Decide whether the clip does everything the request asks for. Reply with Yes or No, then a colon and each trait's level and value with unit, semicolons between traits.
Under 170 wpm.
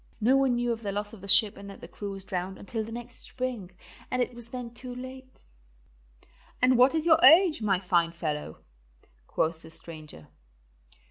No: average, 195 wpm